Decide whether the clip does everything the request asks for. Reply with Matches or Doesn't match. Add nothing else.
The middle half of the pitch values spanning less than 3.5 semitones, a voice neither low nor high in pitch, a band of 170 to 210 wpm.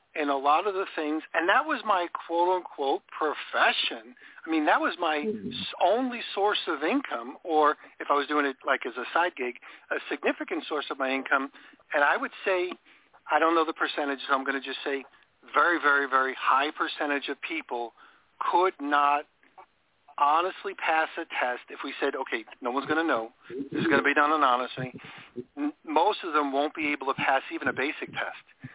Doesn't match